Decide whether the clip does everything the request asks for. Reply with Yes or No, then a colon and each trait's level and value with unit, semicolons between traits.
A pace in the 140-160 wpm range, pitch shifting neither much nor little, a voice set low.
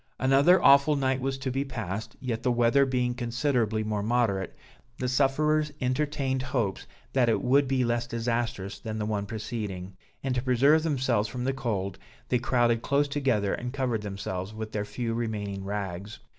No: average, 170 wpm; average, 3.8 semitones; low, 120 Hz